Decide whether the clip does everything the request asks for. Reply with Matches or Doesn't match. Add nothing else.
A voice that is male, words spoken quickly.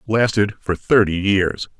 Doesn't match